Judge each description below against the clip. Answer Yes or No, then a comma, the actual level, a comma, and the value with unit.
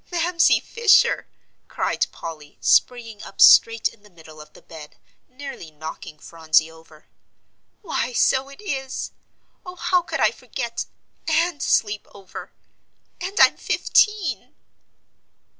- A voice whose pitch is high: Yes, high, 235 Hz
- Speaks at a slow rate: Yes, slow, 125 wpm